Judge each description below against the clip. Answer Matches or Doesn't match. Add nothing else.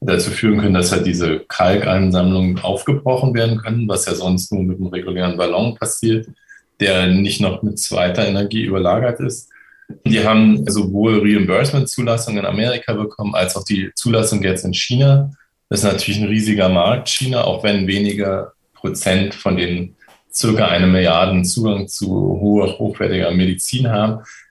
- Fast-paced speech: Doesn't match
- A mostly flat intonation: Doesn't match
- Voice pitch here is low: Matches